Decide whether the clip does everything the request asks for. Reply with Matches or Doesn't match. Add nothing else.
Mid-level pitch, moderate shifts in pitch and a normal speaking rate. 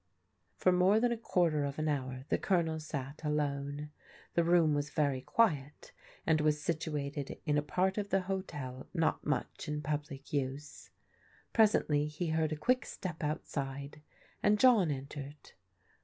Matches